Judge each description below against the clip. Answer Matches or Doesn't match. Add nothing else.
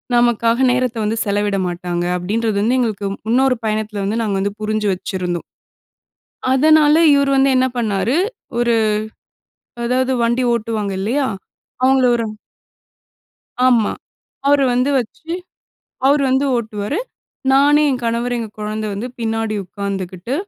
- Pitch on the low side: Doesn't match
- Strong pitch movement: Doesn't match